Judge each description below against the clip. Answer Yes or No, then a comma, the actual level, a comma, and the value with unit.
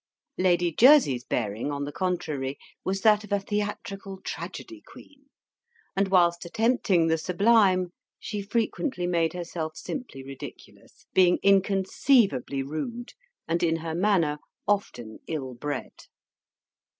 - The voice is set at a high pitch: No, medium, 180 Hz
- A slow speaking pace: Yes, slow, 120 wpm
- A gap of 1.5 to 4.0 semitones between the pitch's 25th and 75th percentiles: No, average, 4.7 semitones